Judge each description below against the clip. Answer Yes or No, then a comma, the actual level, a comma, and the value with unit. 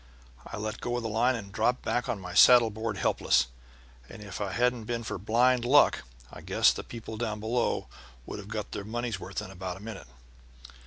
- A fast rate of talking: Yes, fast, 210 wpm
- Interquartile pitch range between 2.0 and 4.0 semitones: Yes, average, 2.9 semitones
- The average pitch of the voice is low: Yes, low, 110 Hz